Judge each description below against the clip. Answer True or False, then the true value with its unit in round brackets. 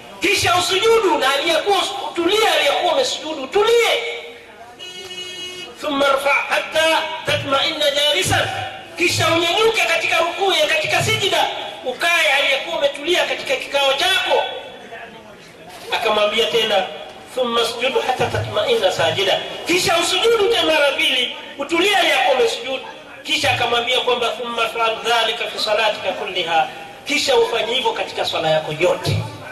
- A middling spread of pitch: False (7.0 semitones)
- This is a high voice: True (290 Hz)